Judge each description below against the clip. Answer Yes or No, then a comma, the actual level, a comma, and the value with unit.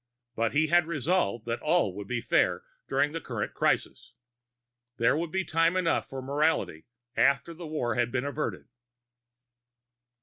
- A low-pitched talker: No, medium, 145 Hz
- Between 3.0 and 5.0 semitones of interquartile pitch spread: No, wide, 5.5 semitones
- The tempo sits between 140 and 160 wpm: Yes, average, 145 wpm